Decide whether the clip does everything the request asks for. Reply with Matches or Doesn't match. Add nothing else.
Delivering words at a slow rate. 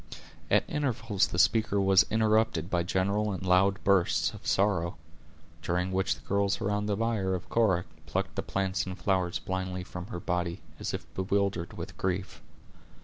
Doesn't match